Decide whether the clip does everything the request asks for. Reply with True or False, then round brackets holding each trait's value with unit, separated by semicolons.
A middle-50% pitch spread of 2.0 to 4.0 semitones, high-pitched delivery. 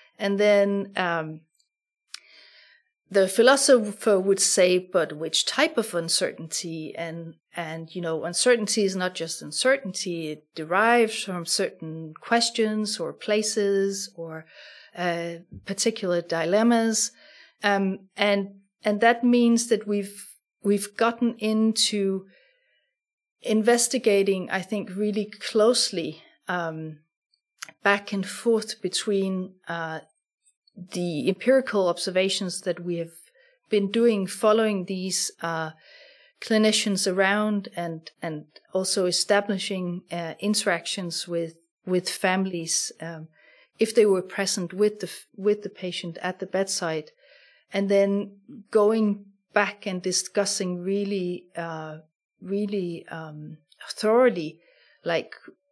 True (3.7 semitones; 195 Hz)